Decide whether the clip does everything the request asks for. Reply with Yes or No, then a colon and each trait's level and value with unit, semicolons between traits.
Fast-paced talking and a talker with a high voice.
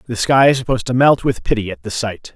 No: fast, 280 wpm; low, 120 Hz